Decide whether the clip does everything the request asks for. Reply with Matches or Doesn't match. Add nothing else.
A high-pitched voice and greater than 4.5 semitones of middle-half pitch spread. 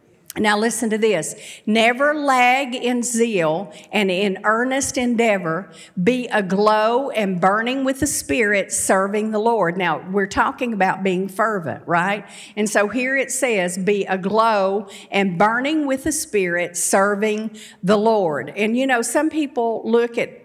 Doesn't match